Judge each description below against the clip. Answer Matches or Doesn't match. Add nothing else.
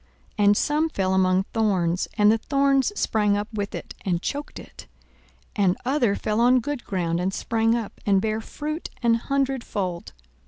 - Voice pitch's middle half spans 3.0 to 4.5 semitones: Doesn't match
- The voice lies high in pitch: Matches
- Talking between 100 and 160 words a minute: Doesn't match